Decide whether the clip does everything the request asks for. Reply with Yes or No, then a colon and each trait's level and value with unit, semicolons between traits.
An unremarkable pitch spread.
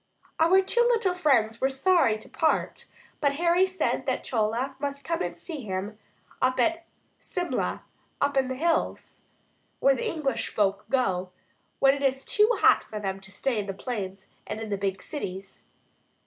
No: wide, 7.5 semitones